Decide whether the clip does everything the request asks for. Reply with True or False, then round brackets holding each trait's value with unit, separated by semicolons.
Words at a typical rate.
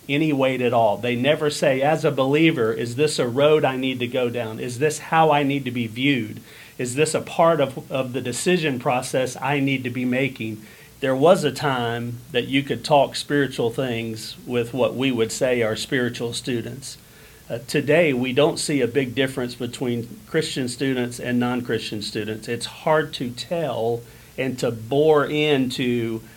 True (185 wpm)